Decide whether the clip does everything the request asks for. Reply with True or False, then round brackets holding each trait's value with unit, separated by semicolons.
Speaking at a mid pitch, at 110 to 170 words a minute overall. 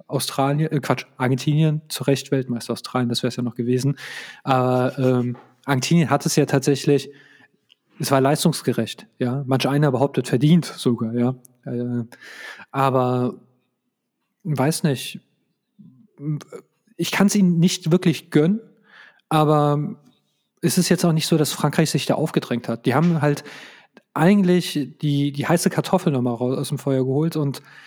True (145 Hz; 155 wpm)